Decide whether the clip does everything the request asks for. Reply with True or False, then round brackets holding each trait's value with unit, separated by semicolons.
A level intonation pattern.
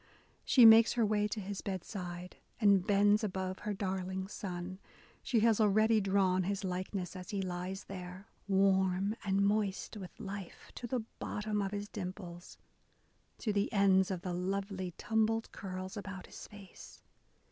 True (1.9 semitones)